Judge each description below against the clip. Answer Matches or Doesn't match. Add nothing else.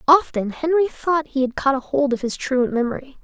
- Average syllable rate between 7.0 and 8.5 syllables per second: Doesn't match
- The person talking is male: Doesn't match